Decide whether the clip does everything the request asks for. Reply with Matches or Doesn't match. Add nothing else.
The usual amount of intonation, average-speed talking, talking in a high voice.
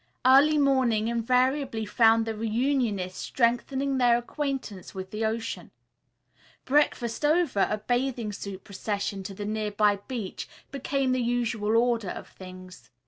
Doesn't match